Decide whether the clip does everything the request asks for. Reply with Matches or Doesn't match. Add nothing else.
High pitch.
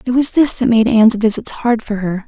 Matches